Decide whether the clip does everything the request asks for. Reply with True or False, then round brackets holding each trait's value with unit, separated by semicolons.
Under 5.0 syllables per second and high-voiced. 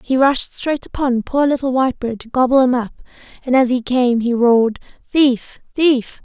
True (4.8 syllables/s; 255 Hz)